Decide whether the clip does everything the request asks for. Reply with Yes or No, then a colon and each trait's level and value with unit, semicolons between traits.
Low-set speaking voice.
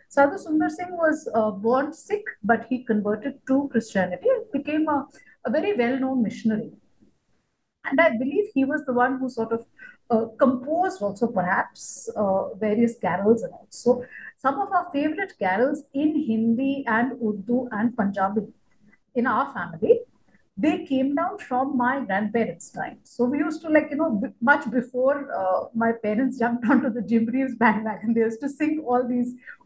No: very high, 250 Hz